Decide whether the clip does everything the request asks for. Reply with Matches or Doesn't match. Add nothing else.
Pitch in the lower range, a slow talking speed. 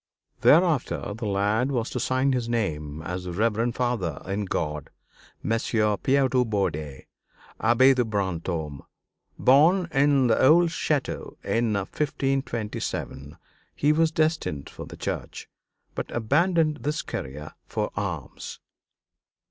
Matches